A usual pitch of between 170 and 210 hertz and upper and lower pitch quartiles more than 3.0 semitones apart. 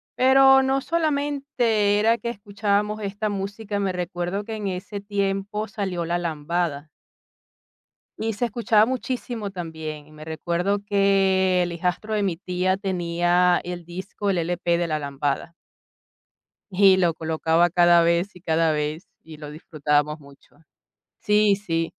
Yes: medium, 185 Hz; average, 3.6 semitones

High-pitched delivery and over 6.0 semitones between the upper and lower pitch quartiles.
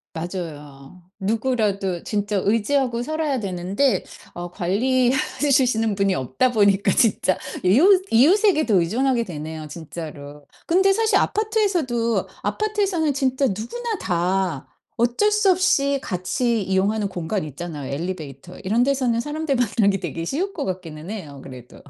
Yes: high, 215 Hz; wide, 7.6 semitones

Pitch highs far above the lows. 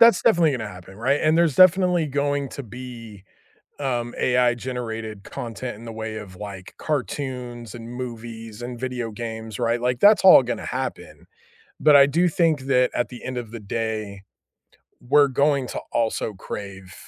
No: average, 4.0 semitones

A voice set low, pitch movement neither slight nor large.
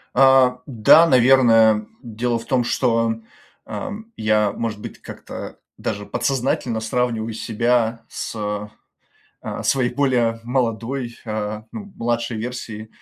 No: low, 115 Hz; narrow, 2.2 semitones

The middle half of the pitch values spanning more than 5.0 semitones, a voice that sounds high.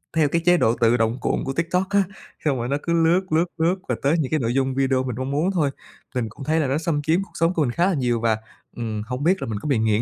No: wide, 5.4 semitones; medium, 140 Hz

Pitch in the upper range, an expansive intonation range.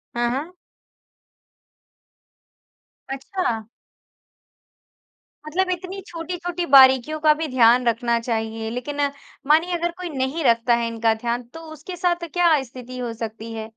Yes: very high, 260 Hz; wide, 6.3 semitones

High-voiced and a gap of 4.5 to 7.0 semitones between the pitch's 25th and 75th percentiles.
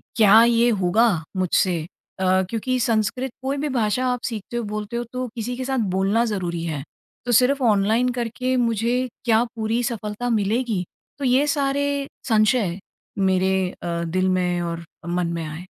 Yes: high, 225 Hz; average, 4.8 semitones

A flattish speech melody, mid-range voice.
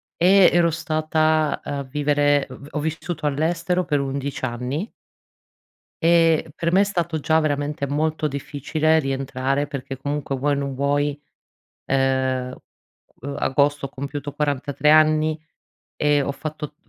Yes: narrow, 2.2 semitones; medium, 145 Hz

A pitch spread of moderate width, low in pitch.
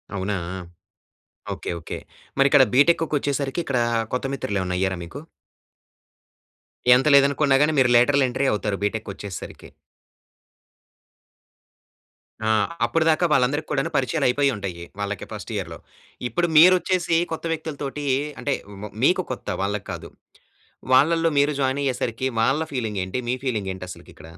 No: wide, 6.0 semitones; low, 130 Hz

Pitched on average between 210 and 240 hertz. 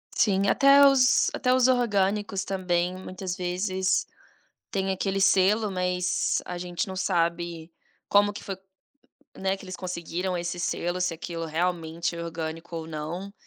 No: medium, 185 Hz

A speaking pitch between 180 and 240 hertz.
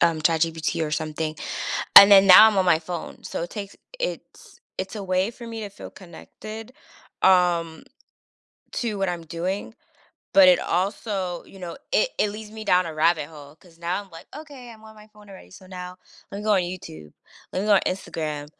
Yes: medium, 185 Hz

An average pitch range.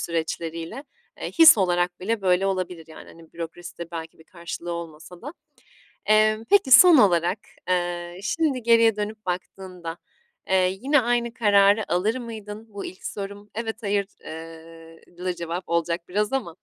Yes: average, 4.2 semitones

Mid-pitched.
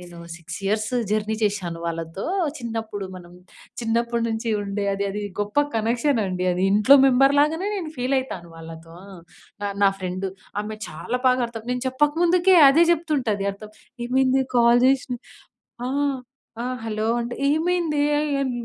No: high, 230 Hz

